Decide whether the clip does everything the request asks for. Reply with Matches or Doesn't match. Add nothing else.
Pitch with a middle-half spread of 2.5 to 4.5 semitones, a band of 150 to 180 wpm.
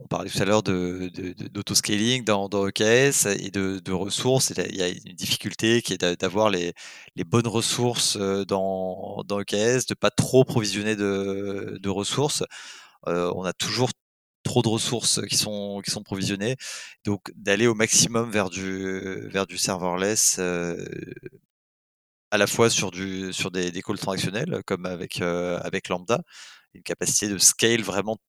Matches